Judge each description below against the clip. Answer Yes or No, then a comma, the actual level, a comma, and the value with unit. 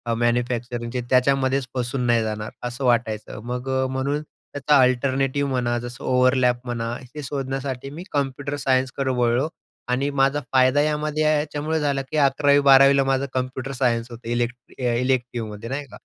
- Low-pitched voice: Yes, low, 130 Hz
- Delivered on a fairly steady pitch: Yes, narrow, 2.2 semitones